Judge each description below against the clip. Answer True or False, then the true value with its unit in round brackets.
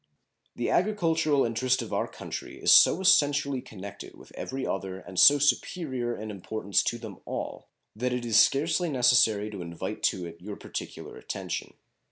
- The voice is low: True (120 Hz)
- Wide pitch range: True (5.7 semitones)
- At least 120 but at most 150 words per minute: False (165 wpm)